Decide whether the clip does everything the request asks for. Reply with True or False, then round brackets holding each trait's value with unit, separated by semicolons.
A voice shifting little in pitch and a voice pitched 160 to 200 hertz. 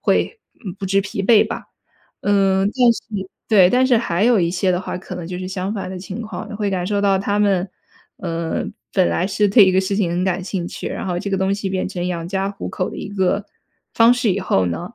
True (2.1 semitones; 195 Hz)